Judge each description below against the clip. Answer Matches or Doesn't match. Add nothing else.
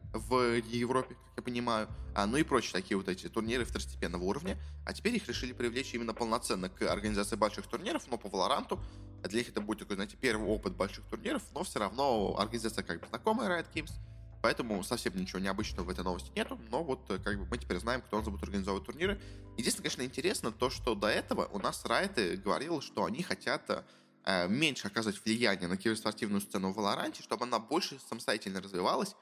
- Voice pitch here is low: Matches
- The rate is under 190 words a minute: Doesn't match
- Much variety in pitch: Doesn't match